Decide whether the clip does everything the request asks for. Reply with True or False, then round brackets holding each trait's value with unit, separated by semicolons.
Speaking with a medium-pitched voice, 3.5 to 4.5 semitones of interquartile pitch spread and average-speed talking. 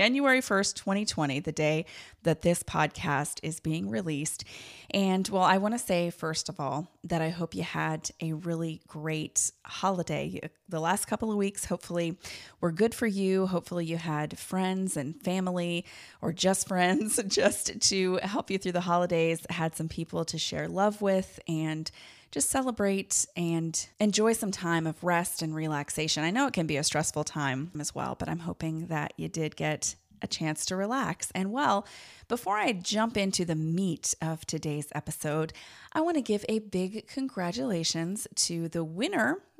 True (170 Hz; 3.9 semitones; 175 wpm)